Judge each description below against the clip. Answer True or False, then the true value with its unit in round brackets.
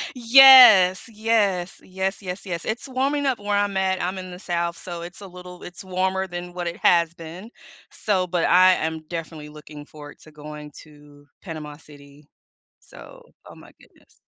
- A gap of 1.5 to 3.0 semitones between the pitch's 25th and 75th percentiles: False (3.4 semitones)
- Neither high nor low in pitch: True (180 Hz)